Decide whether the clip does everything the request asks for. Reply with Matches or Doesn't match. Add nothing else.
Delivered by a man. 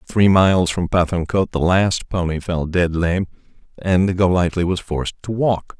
Matches